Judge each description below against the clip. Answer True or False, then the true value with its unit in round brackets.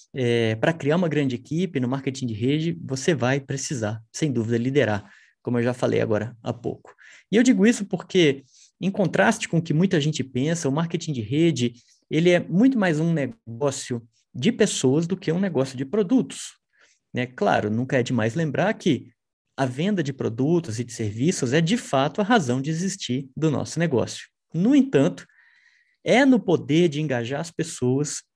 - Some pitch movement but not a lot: False (6.0 semitones)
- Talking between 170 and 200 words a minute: True (185 wpm)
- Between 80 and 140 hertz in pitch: False (150 Hz)